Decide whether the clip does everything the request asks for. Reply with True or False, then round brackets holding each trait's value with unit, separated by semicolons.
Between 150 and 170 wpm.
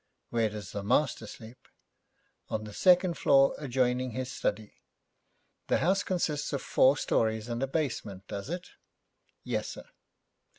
False (140 wpm)